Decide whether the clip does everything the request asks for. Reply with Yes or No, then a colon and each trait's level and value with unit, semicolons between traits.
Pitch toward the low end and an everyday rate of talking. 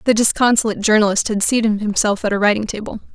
No: high, 215 Hz; average, 190 wpm